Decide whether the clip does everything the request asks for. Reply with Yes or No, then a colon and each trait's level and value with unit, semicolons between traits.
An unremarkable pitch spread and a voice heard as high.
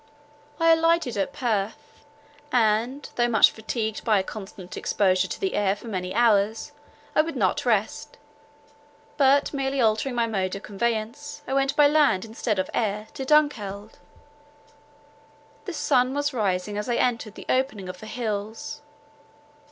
Yes: average, 4.7 semitones; high, 225 Hz